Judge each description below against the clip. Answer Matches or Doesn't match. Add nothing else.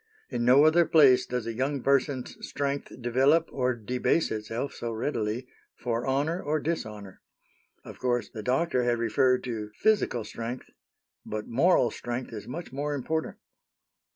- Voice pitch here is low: Matches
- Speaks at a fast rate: Doesn't match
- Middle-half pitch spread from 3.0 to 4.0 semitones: Matches